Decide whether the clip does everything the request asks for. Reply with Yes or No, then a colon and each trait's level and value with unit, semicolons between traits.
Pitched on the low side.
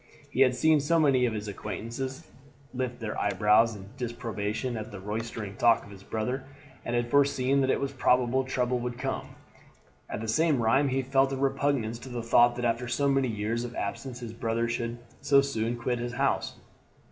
Yes: low, 120 Hz